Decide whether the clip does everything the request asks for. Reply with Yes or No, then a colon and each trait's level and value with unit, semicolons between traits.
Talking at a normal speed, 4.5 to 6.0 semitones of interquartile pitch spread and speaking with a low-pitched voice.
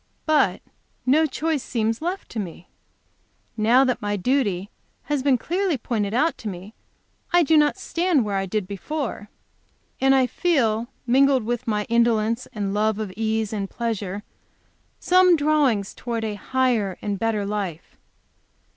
No: average, 150 wpm; average, 5.0 semitones; high, 230 Hz